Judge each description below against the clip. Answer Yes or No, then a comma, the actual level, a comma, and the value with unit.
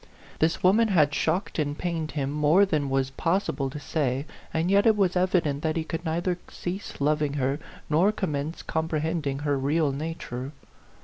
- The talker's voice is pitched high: No, medium, 155 Hz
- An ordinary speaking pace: Yes, average, 175 wpm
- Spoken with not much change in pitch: No, average, 3.5 semitones